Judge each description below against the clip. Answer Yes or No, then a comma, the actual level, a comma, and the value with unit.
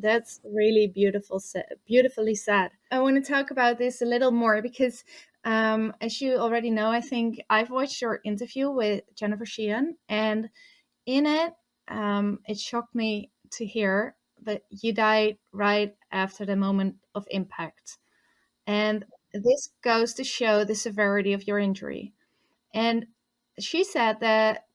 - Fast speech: No, average, 150 wpm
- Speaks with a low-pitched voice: No, high, 220 Hz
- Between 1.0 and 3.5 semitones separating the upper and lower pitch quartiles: Yes, average, 3.0 semitones